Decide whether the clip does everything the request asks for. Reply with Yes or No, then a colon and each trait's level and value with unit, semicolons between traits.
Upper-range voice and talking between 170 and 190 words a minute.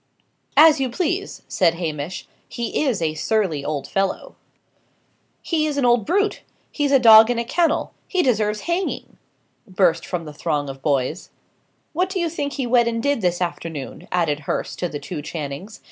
Yes: high, 215 Hz; average, 175 wpm